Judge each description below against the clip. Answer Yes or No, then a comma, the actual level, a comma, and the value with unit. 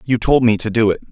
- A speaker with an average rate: No, fast, 320 wpm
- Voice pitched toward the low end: Yes, low, 115 Hz